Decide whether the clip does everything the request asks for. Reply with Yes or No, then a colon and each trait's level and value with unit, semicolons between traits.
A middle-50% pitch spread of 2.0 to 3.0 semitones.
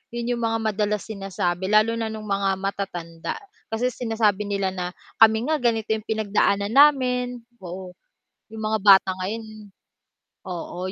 Yes: average, 2.7 semitones